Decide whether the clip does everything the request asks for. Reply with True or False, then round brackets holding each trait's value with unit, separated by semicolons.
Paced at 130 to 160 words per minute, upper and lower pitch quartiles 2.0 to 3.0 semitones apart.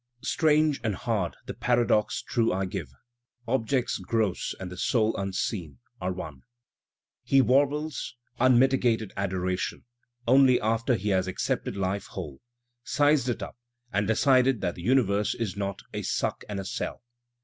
False (150 wpm; 5.2 semitones)